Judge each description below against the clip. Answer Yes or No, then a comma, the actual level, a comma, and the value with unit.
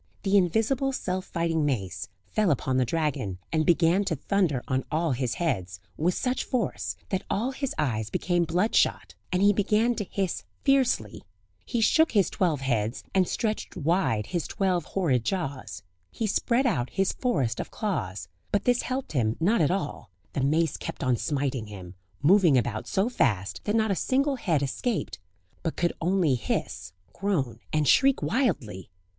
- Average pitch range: No, wide, 8.1 semitones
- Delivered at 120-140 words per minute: No, average, 170 wpm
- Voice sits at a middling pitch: Yes, medium, 170 Hz